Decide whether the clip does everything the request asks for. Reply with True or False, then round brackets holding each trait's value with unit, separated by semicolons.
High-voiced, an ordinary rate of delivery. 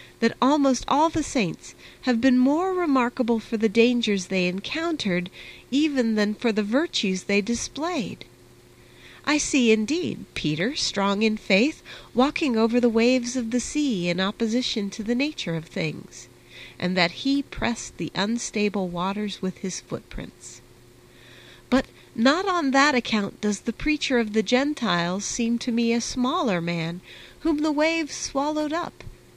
True (230 Hz; 150 wpm)